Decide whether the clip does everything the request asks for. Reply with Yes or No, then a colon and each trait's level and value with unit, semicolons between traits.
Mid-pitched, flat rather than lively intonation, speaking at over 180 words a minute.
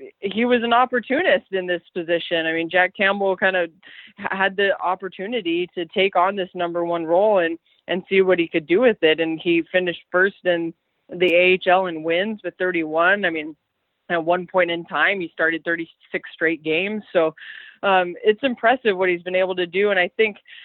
Yes: medium, 180 Hz; narrow, 2.3 semitones; average, 200 wpm